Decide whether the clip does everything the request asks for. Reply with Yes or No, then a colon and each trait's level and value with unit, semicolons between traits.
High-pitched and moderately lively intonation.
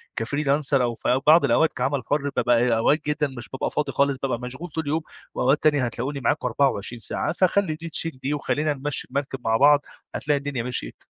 No: medium, 140 Hz; average, 3.1 semitones